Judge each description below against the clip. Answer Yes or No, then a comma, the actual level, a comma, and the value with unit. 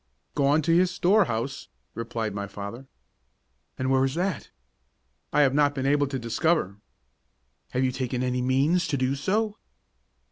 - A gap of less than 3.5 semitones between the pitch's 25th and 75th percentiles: No, average, 4.1 semitones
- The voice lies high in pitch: No, low, 135 Hz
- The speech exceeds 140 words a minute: Yes, average, 150 wpm